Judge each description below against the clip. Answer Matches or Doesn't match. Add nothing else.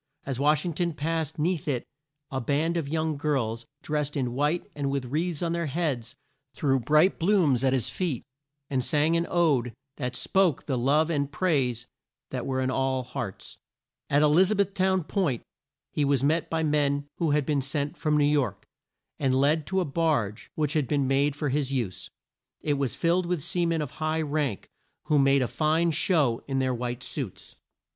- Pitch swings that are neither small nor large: Matches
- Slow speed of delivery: Doesn't match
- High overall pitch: Doesn't match